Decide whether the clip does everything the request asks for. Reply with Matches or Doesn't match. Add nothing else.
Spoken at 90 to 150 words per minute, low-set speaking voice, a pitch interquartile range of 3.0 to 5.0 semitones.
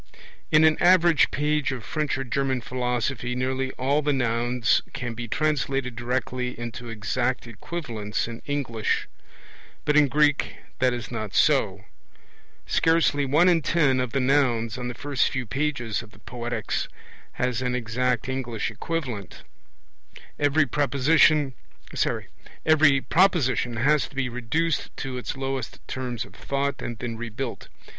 Matches